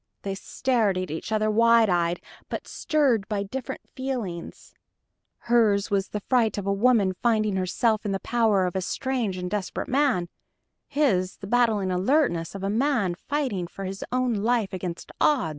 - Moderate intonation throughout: Yes, average, 4.3 semitones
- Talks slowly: No, average, 170 wpm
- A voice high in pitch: Yes, high, 210 Hz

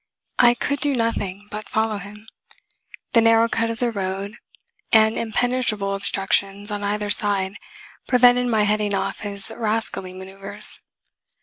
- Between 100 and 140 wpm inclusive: Yes, slow, 135 wpm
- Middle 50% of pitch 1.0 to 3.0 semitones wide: Yes, narrow, 2.4 semitones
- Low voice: No, high, 210 Hz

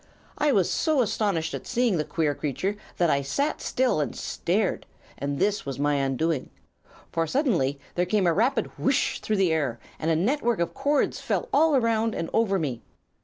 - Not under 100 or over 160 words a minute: No, average, 185 wpm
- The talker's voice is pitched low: No, medium, 185 Hz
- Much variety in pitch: Yes, wide, 7.8 semitones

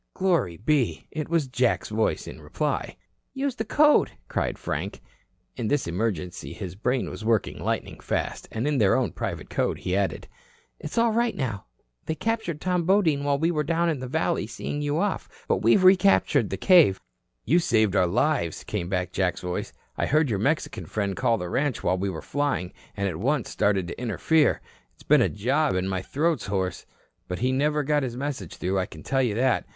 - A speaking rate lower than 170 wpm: No, average, 200 wpm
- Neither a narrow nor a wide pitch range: No, wide, 7.8 semitones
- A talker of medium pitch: No, low, 130 Hz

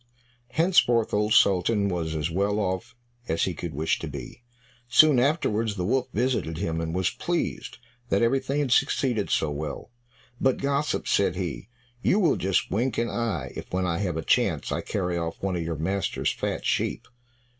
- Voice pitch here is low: Yes, low, 100 Hz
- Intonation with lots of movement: Yes, wide, 6.3 semitones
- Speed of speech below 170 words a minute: No, average, 180 wpm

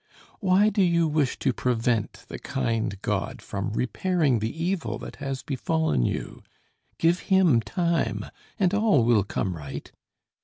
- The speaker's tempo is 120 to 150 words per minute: Yes, average, 145 wpm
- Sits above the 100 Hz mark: Yes, medium, 140 Hz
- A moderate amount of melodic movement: No, wide, 7.8 semitones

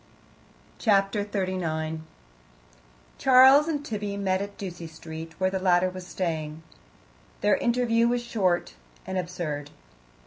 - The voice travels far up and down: No, average, 4.2 semitones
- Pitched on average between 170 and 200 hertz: Yes, medium, 185 Hz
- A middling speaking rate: No, slow, 115 wpm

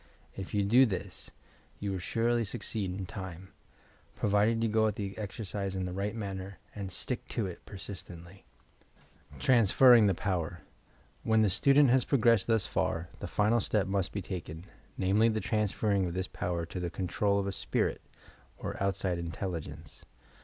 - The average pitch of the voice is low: Yes, low, 100 Hz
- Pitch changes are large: No, average, 2.9 semitones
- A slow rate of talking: No, average, 165 wpm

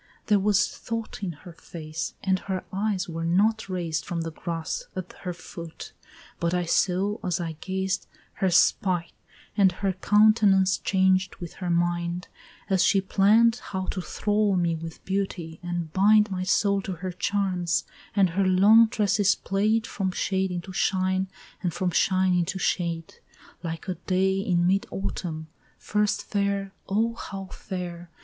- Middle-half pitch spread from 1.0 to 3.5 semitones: Yes, narrow, 2.4 semitones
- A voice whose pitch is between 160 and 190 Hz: Yes, medium, 185 Hz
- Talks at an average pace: Yes, average, 155 wpm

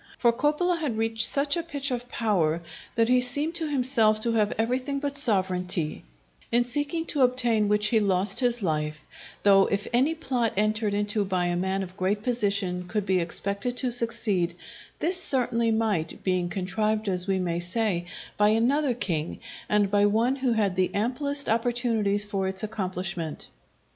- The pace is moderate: Yes, average, 170 wpm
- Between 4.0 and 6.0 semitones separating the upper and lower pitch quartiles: Yes, average, 4.5 semitones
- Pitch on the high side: Yes, high, 215 Hz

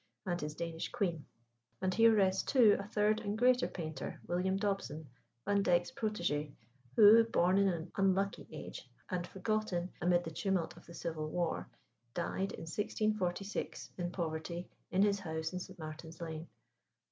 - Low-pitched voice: No, medium, 180 Hz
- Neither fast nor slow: Yes, average, 155 wpm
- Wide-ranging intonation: No, average, 3.3 semitones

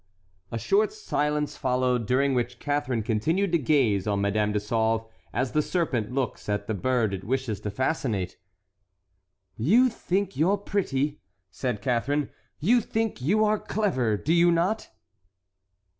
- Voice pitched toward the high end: No, low, 130 Hz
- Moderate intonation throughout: No, wide, 7.3 semitones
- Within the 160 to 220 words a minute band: No, average, 150 wpm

